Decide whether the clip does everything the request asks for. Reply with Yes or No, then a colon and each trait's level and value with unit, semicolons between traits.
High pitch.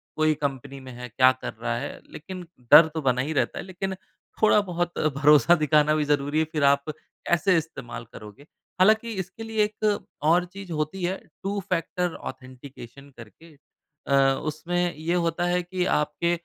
No: medium, 160 Hz